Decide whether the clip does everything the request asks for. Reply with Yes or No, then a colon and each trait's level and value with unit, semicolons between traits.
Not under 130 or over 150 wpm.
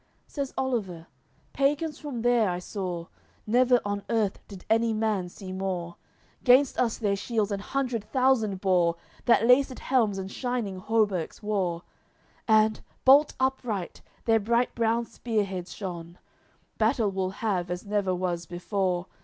Yes: average, 145 wpm